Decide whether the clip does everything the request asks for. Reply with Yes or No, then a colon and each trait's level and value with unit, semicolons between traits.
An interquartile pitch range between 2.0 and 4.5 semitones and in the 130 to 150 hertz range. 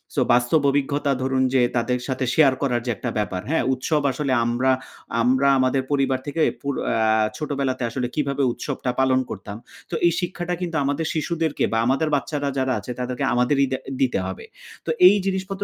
Yes: average, 2.8 semitones; low, 135 Hz